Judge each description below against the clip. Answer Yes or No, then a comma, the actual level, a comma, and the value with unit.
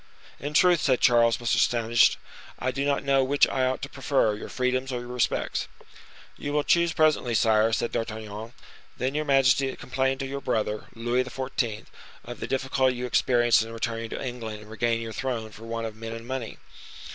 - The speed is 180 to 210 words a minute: Yes, average, 190 wpm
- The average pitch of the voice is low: Yes, low, 125 Hz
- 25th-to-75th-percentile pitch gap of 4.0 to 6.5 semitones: No, average, 2.7 semitones